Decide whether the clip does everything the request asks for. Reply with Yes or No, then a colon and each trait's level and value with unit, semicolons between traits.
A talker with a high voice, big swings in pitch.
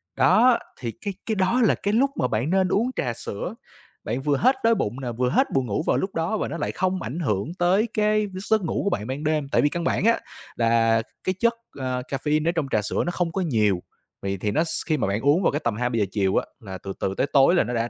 No: medium, 145 Hz; wide, 8.4 semitones